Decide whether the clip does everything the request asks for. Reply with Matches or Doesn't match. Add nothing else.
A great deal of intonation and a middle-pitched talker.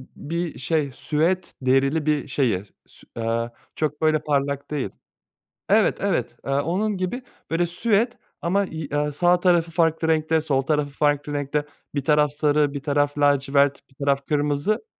Doesn't match